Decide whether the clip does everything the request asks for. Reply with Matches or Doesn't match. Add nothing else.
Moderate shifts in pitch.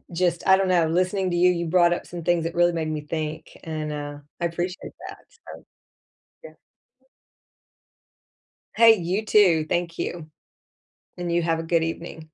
Doesn't match